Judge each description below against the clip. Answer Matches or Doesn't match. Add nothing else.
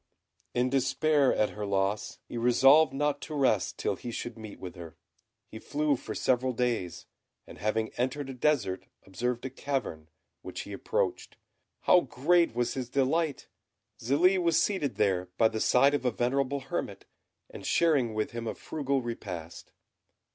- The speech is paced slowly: Doesn't match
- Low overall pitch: Matches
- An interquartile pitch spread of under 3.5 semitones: Doesn't match